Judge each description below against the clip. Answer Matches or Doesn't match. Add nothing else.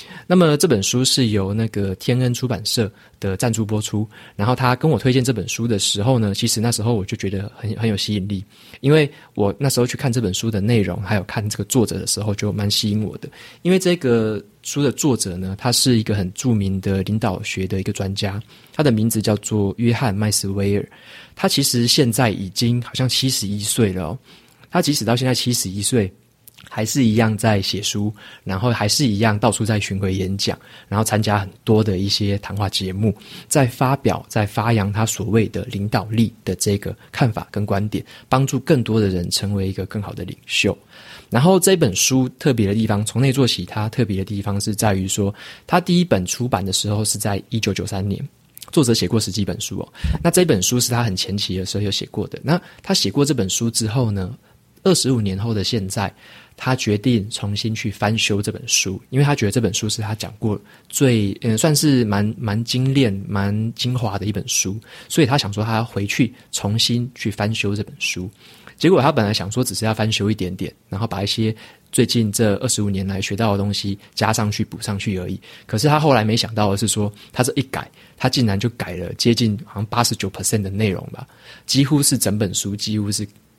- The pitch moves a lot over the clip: Doesn't match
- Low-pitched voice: Matches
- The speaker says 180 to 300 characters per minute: Doesn't match